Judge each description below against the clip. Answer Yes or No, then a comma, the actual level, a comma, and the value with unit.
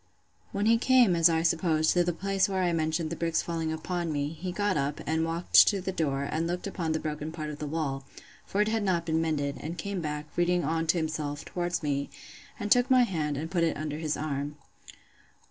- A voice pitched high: No, medium, 165 Hz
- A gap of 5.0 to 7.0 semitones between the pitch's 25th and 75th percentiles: No, average, 2.7 semitones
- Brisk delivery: Yes, fast, 230 wpm